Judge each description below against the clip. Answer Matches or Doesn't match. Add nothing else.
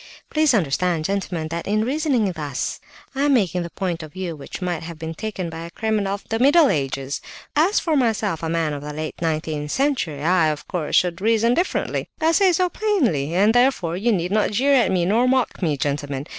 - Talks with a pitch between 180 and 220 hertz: Matches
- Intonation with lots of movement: Matches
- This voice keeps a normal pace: Doesn't match